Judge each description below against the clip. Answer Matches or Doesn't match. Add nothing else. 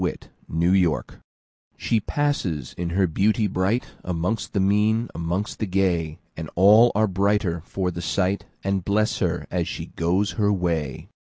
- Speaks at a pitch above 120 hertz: Doesn't match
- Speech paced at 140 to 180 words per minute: Matches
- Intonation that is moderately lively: Matches